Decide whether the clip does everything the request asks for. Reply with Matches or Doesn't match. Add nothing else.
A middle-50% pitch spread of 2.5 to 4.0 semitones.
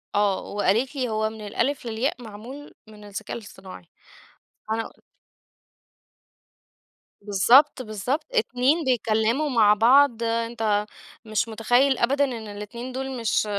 Matches